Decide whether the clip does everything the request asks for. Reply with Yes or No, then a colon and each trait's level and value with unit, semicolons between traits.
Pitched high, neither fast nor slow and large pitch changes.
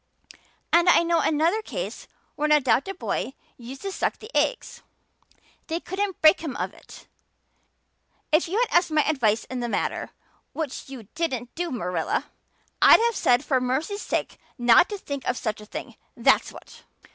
Yes: very high, 305 Hz; average, 170 wpm; wide, 5.9 semitones